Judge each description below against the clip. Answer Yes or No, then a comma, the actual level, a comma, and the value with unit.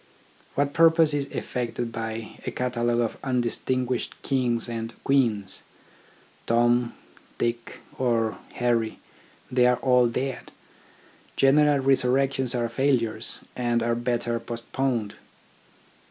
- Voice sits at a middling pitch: No, low, 120 Hz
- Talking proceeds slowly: Yes, slow, 110 wpm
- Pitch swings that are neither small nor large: No, narrow, 2.2 semitones